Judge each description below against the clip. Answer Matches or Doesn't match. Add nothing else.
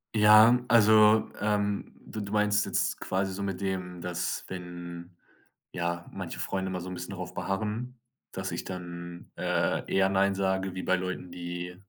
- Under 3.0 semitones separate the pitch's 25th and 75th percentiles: Matches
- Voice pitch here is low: Matches